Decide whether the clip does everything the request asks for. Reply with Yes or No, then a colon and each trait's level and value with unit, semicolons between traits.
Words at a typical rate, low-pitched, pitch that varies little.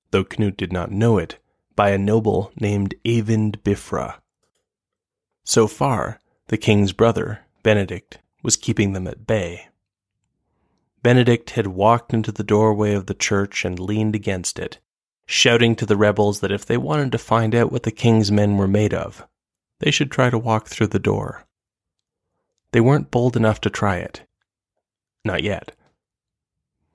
Yes: average, 160 wpm; low, 110 Hz; narrow, 2.2 semitones